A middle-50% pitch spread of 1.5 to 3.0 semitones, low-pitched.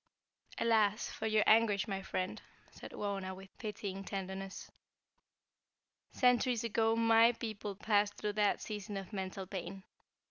No: narrow, 2.4 semitones; high, 205 Hz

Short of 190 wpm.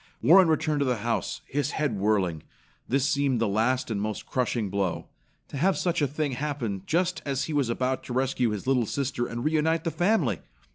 No: average, 200 wpm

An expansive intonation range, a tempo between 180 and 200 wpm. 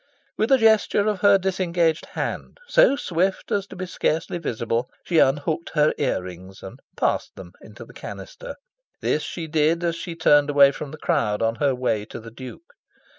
Yes: wide, 6.6 semitones; average, 185 wpm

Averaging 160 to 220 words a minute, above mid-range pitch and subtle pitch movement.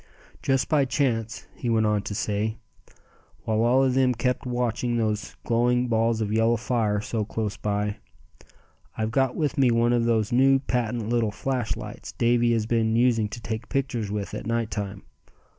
No: average, 175 wpm; low, 115 Hz; narrow, 2.1 semitones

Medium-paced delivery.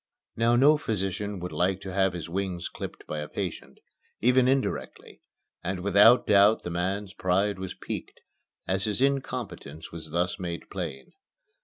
Yes: average, 155 wpm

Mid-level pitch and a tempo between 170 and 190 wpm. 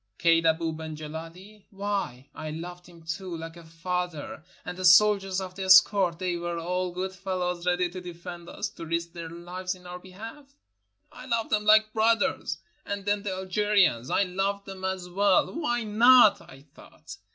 Yes: medium, 180 Hz; average, 180 wpm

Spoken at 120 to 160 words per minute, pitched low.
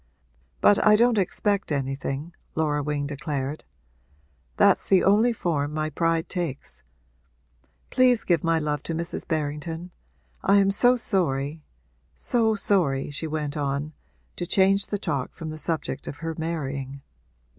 No: average, 140 wpm; medium, 160 Hz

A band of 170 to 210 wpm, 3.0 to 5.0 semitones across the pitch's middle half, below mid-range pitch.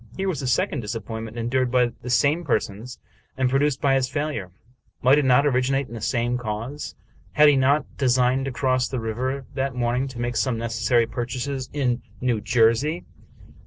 No: average, 185 wpm; narrow, 2.5 semitones; low, 125 Hz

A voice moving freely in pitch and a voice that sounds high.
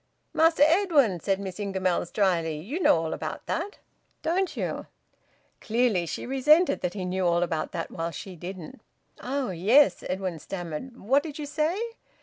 Yes: wide, 8.5 semitones; high, 200 Hz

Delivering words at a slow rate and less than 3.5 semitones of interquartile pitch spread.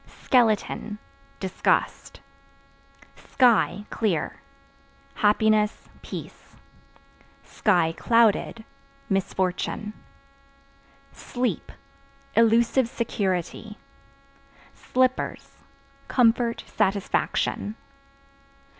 Yes: slow, 45 wpm; average, 2.7 semitones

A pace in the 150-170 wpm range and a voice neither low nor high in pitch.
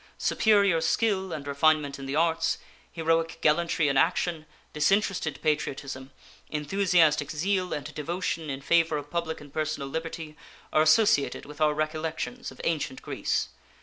No: average, 140 wpm; medium, 160 Hz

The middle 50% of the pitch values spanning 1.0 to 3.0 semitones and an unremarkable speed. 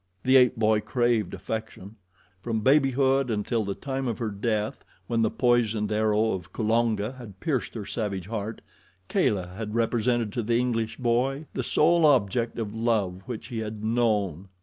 Yes: narrow, 2.4 semitones; average, 165 wpm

